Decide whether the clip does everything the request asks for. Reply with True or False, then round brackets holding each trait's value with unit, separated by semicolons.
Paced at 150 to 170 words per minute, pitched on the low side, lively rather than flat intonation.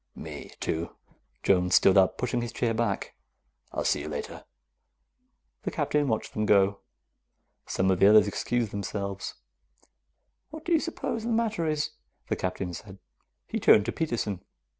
True (155 wpm; 105 Hz; 7.1 semitones)